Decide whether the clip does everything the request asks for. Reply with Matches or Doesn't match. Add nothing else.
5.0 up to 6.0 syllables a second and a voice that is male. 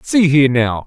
Matches